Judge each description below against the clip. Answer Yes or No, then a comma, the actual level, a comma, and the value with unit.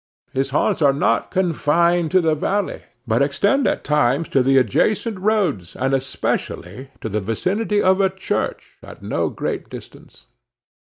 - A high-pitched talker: No, medium, 150 Hz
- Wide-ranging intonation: Yes, wide, 6.2 semitones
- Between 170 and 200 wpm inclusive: No, average, 155 wpm